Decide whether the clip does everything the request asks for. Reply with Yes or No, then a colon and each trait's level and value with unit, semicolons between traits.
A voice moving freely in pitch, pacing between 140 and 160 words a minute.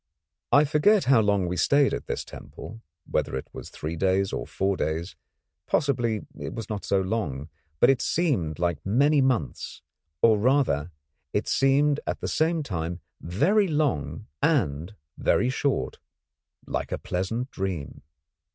Yes: wide, 8.2 semitones; average, 150 wpm